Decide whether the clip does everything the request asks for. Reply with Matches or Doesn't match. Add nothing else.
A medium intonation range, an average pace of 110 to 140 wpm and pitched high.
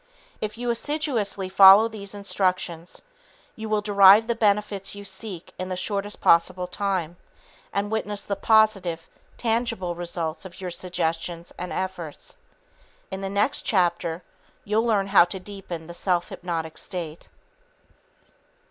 Matches